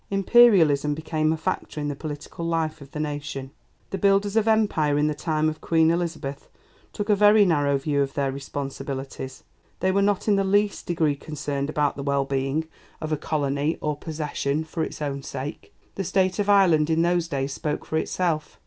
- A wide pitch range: No, average, 3.9 semitones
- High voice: No, medium, 155 Hz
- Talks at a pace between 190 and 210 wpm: Yes, average, 195 wpm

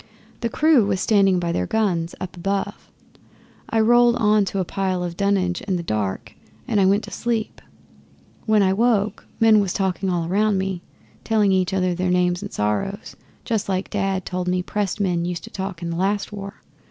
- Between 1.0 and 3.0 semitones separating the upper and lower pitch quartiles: Yes, average, 2.7 semitones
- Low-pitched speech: No, high, 195 Hz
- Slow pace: No, average, 195 wpm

